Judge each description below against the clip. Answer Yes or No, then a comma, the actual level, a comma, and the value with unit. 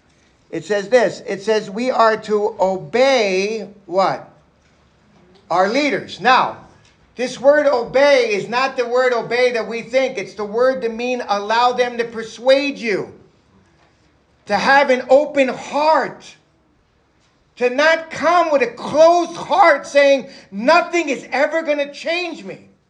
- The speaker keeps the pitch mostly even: No, average, 4.2 semitones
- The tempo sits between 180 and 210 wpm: No, average, 140 wpm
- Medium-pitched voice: No, very high, 250 Hz